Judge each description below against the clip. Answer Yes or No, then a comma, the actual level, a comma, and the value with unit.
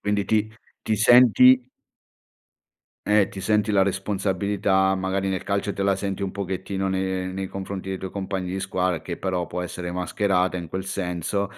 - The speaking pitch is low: Yes, very low, 95 Hz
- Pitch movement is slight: Yes, narrow, 1.4 semitones